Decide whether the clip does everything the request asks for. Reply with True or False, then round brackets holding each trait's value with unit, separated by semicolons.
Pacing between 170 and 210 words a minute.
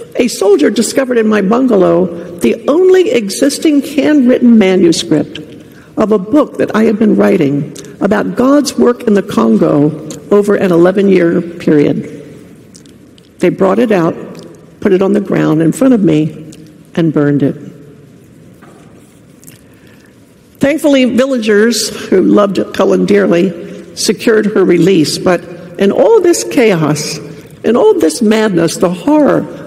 False (135 wpm)